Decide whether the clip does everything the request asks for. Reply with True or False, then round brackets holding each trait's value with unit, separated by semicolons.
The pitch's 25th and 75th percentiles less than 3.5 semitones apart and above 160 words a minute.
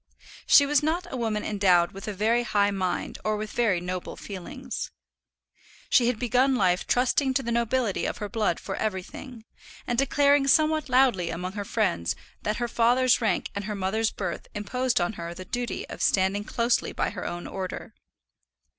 False (4.6 semitones; 180 wpm)